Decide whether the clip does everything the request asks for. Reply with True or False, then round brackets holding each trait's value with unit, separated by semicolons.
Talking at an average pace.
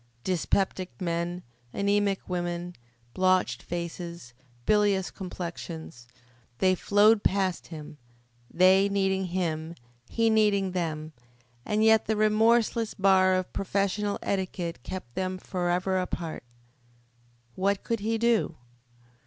False (105 wpm)